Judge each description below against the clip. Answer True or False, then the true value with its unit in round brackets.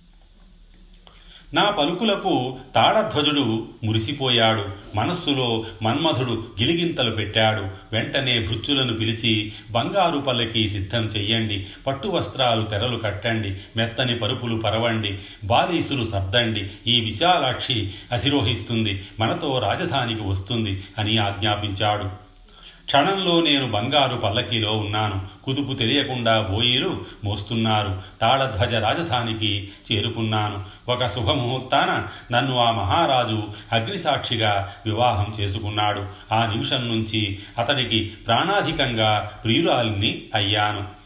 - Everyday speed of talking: True (85 wpm)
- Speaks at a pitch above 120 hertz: False (110 Hz)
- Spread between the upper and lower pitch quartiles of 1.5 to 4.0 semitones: True (2.7 semitones)